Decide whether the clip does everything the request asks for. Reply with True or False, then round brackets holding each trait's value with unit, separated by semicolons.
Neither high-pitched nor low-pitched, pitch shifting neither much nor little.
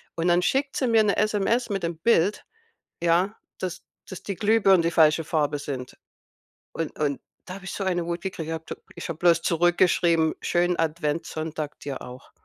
True (170 Hz; 3.3 semitones)